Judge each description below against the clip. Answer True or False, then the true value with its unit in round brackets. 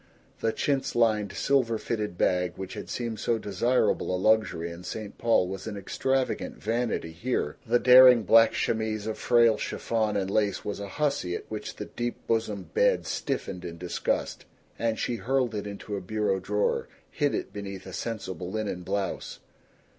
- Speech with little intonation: False (3.2 semitones)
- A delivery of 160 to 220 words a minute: True (170 wpm)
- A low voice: True (110 Hz)